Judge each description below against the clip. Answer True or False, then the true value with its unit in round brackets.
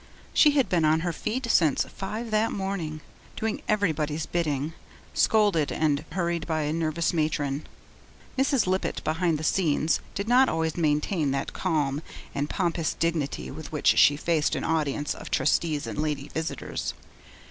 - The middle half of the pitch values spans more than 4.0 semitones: False (3.7 semitones)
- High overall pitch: False (160 Hz)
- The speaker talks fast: False (155 wpm)